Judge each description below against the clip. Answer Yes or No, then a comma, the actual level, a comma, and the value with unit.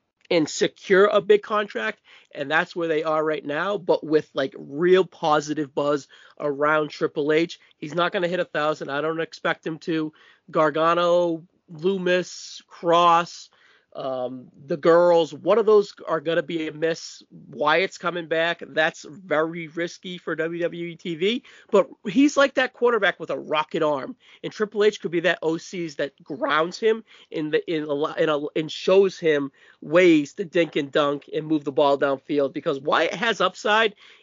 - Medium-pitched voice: Yes, medium, 165 Hz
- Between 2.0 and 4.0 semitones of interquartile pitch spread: Yes, average, 3.4 semitones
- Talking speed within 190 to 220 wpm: No, average, 180 wpm